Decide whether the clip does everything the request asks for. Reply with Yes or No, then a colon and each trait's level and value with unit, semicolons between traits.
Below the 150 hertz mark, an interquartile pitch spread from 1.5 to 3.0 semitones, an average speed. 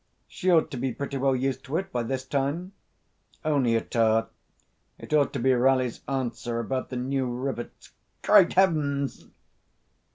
Yes: low, 135 Hz; narrow, 2.4 semitones; average, 160 wpm